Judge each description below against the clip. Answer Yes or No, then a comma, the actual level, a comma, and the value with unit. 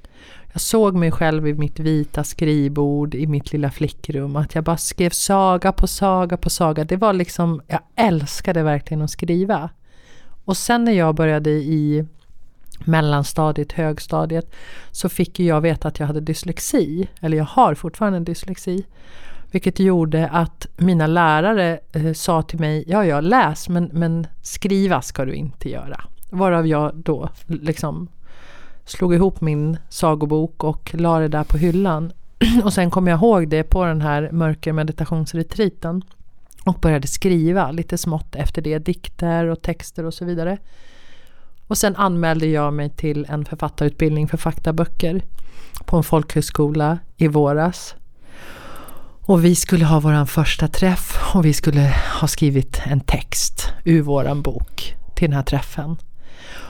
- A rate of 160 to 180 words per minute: No, average, 150 wpm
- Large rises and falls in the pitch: No, average, 2.7 semitones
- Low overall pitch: No, medium, 160 Hz